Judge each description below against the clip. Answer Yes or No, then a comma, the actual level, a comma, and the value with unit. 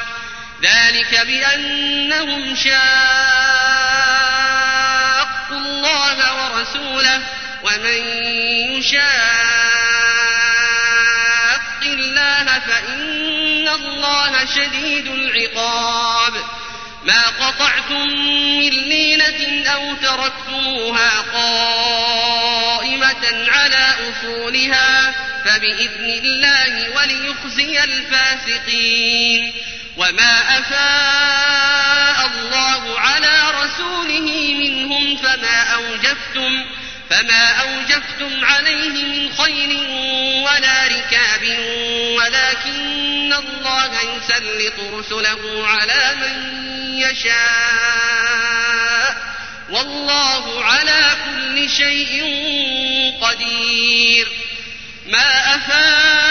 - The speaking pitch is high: Yes, very high, 265 Hz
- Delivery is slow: Yes, slow, 60 wpm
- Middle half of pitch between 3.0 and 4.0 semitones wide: Yes, average, 3.4 semitones